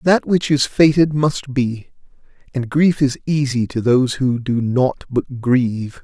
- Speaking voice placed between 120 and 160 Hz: Yes, low, 135 Hz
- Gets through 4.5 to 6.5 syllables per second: No, 4.1 syllables/s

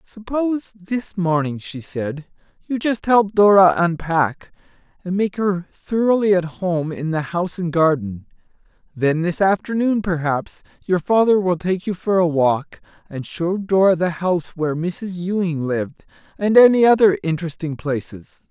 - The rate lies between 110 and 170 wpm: Yes, average, 150 wpm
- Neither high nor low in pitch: Yes, medium, 180 Hz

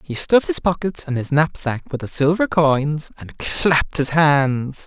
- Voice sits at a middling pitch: Yes, medium, 150 Hz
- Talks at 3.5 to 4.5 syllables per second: Yes, 4.4 syllables/s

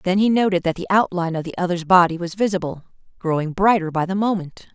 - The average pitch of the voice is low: No, medium, 180 Hz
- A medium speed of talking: No, fast, 215 wpm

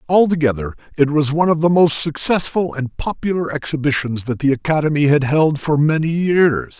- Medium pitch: Yes, medium, 150 Hz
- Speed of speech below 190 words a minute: Yes, average, 170 wpm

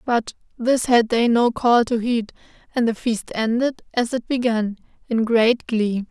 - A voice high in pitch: Yes, high, 235 Hz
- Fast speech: No, average, 175 wpm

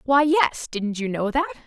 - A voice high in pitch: Yes, very high, 255 Hz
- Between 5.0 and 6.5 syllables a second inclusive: No, 4.4 syllables/s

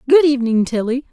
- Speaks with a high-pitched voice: Yes, very high, 260 Hz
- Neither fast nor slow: Yes, average, 160 wpm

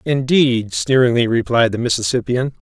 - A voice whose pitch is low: Yes, low, 125 Hz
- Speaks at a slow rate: Yes, slow, 110 wpm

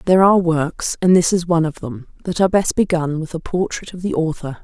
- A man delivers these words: No, female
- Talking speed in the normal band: No, fast, 245 wpm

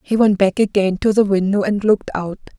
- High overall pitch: Yes, high, 200 Hz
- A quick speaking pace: Yes, fast, 230 wpm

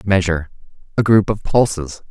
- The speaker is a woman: No, male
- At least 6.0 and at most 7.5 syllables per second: No, 5.3 syllables/s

